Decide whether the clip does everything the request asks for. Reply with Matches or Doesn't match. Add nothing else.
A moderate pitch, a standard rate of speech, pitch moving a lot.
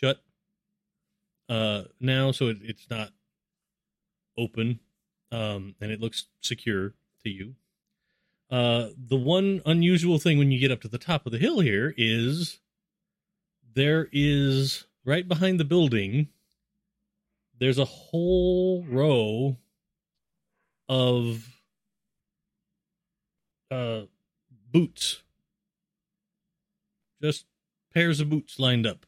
Doesn't match